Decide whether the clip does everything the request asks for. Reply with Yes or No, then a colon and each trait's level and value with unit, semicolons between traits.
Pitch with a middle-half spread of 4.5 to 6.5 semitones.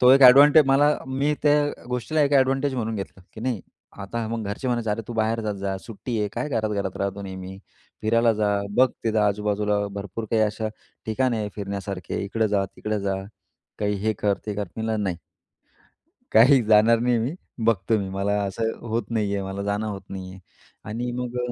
No: average, 3.2 semitones